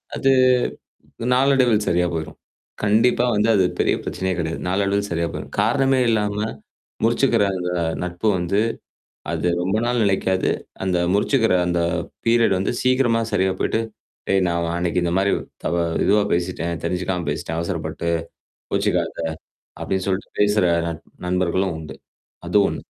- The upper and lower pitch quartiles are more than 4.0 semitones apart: No, average, 3.7 semitones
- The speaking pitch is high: No, very low, 95 Hz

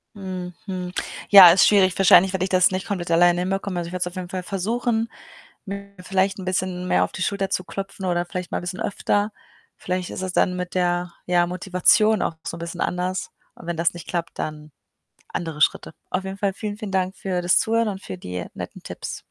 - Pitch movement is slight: Yes, narrow, 1.7 semitones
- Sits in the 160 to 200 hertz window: Yes, medium, 185 Hz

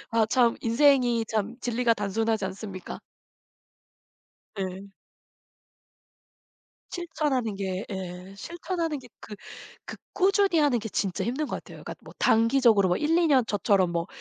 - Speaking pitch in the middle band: No, high, 230 Hz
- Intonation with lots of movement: Yes, wide, 5.8 semitones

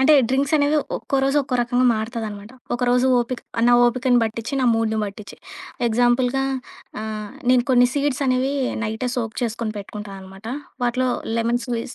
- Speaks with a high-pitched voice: Yes, high, 240 Hz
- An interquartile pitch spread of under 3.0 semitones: Yes, narrow, 2.6 semitones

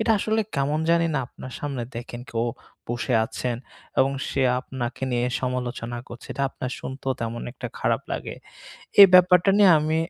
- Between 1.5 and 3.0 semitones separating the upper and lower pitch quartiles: No, average, 4.4 semitones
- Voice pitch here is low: Yes, low, 130 Hz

